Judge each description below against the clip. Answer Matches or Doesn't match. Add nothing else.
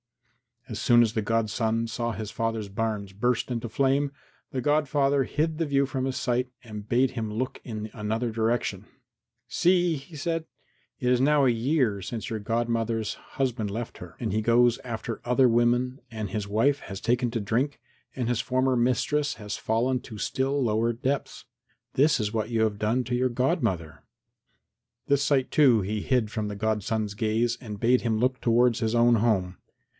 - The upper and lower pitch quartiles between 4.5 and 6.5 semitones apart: Doesn't match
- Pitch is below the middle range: Matches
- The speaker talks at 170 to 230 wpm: Matches